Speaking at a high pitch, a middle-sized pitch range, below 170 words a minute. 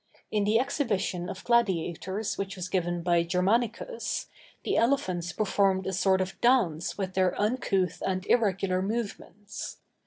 Yes: high, 195 Hz; average, 3.1 semitones; slow, 135 wpm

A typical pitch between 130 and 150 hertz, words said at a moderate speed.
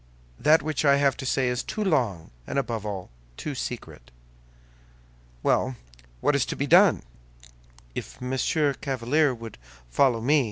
Yes: low, 135 Hz; average, 150 wpm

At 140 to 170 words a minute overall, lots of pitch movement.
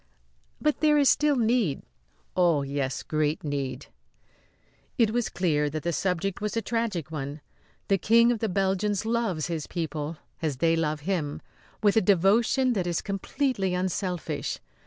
Yes: average, 155 wpm; wide, 6.2 semitones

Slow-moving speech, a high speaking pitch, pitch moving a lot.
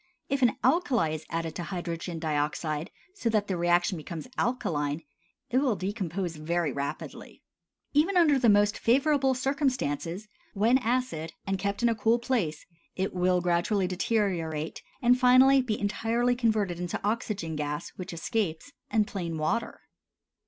No: average, 145 wpm; high, 200 Hz; wide, 6.5 semitones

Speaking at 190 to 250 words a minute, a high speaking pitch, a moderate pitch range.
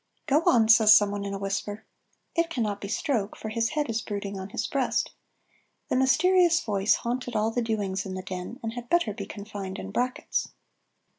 Yes: average, 195 wpm; high, 220 Hz; average, 3.6 semitones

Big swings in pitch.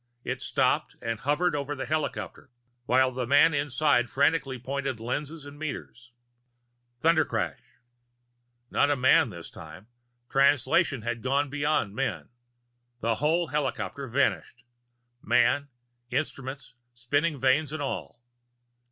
No: average, 2.9 semitones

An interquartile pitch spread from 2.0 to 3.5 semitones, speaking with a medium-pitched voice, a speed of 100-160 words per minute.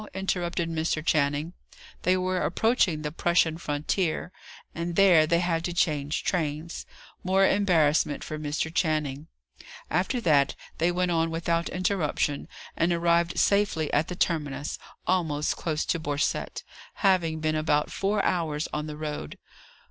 Yes: average, 2.8 semitones; medium, 165 Hz; average, 140 wpm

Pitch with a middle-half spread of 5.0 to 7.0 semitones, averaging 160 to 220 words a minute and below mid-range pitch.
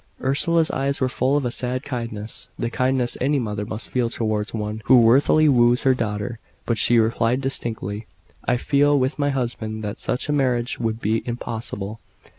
No: average, 3.2 semitones; average, 180 wpm; low, 120 Hz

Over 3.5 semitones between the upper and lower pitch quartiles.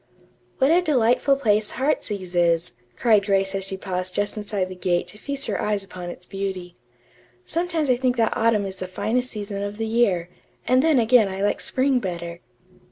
Yes: average, 4.8 semitones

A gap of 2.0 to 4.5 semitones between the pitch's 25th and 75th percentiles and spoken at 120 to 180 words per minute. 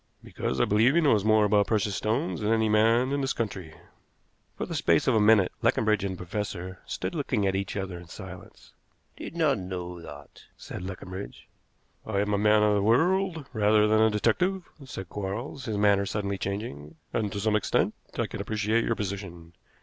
No: average, 2.7 semitones; average, 195 wpm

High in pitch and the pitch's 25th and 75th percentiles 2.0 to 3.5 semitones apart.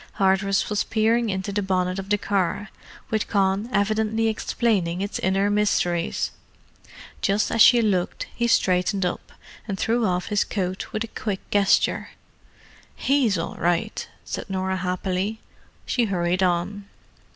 Yes: high, 200 Hz; narrow, 2.6 semitones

